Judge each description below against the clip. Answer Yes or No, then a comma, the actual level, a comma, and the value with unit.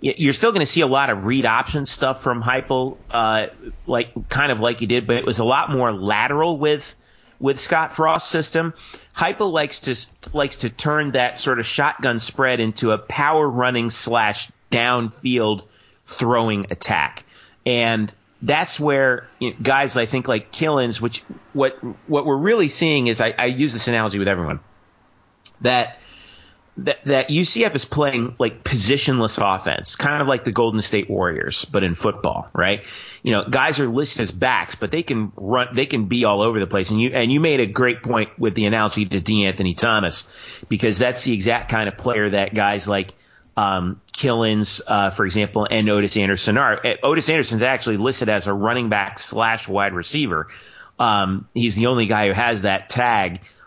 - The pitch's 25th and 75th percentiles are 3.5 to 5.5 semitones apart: Yes, average, 3.9 semitones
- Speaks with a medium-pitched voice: No, low, 120 Hz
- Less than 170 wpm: No, average, 185 wpm